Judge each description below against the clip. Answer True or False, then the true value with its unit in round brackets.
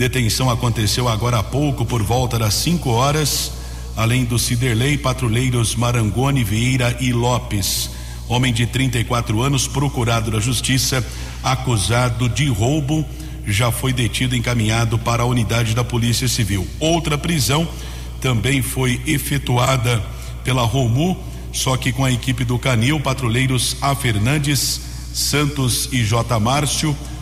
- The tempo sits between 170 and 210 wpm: False (130 wpm)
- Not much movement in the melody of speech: True (2.3 semitones)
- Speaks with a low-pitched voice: True (125 Hz)